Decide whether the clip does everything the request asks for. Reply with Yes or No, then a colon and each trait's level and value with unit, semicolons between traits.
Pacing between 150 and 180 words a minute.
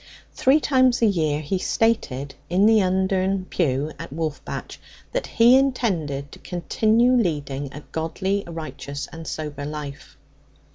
No: slow, 135 wpm